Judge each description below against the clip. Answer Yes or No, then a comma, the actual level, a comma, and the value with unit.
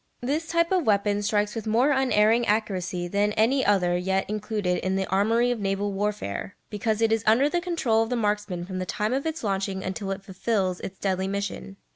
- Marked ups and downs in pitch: No, average, 2.9 semitones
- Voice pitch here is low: No, high, 210 Hz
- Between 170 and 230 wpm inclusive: Yes, fast, 205 wpm